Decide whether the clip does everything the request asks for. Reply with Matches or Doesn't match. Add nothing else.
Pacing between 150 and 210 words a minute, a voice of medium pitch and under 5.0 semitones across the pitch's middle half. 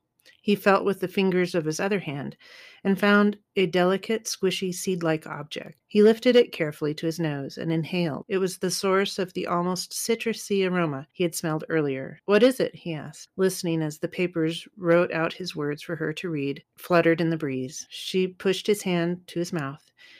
Matches